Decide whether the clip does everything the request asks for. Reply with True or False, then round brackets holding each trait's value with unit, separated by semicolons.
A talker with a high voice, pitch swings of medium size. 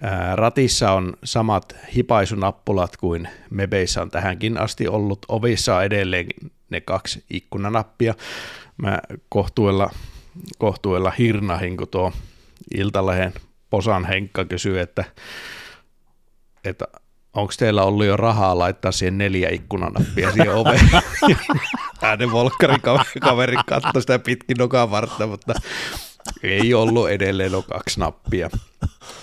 False (100 Hz; 3.3 semitones)